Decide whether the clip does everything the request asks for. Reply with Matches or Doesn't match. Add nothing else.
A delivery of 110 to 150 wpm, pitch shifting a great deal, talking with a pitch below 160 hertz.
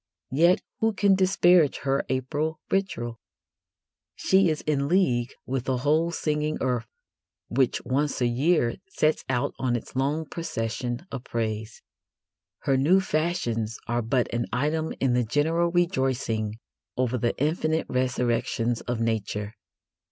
Doesn't match